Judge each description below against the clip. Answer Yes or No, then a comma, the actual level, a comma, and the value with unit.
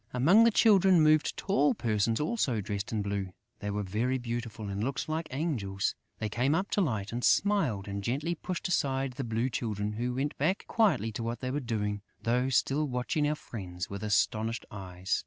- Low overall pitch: Yes, low, 120 Hz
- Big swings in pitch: Yes, wide, 6.0 semitones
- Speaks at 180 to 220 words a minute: Yes, average, 195 wpm